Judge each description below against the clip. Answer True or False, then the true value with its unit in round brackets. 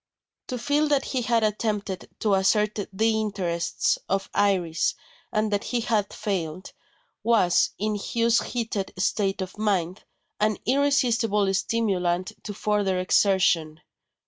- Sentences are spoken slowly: True (125 wpm)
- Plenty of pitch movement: False (3.0 semitones)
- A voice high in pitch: True (210 Hz)